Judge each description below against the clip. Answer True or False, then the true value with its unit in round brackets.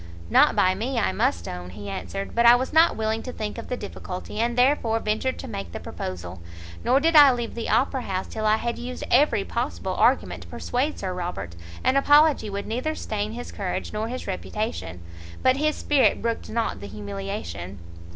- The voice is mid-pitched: False (220 Hz)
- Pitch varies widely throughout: True (5.9 semitones)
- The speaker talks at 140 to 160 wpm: False (200 wpm)